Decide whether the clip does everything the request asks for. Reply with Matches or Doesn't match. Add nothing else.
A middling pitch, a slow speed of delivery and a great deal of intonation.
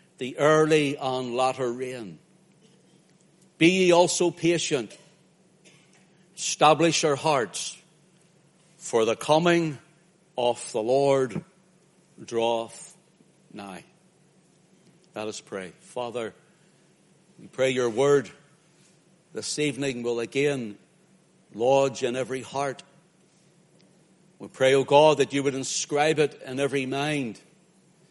Doesn't match